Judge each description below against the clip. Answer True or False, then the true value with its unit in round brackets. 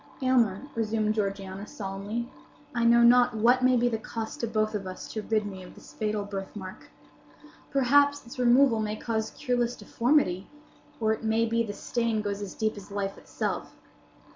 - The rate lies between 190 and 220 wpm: False (175 wpm)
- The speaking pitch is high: True (220 Hz)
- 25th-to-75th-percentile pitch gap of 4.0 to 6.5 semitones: False (2.7 semitones)